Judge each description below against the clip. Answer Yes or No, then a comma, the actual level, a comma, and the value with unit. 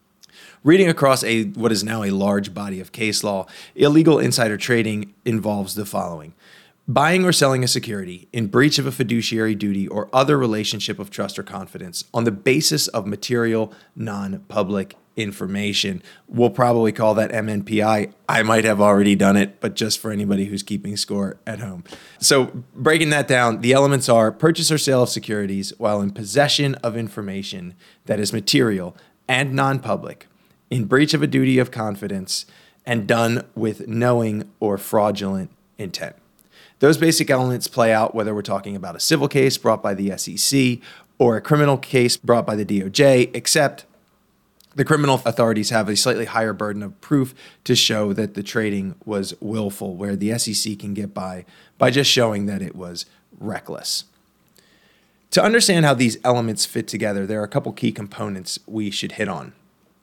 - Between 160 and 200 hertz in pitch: No, low, 110 Hz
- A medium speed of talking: Yes, average, 170 wpm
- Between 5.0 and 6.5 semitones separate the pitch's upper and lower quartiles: No, average, 3.8 semitones